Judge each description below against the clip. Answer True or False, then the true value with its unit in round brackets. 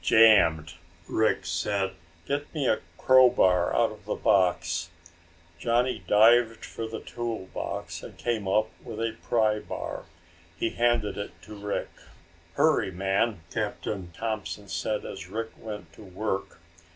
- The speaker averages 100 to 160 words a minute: True (140 wpm)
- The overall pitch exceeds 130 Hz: False (105 Hz)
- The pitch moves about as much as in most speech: True (3.2 semitones)